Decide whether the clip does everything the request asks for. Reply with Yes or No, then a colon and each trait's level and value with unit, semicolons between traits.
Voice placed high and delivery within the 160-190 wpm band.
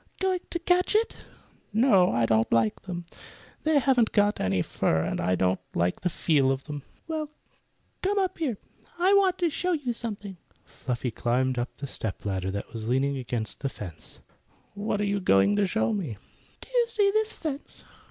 Yes: high, 195 Hz; average, 185 wpm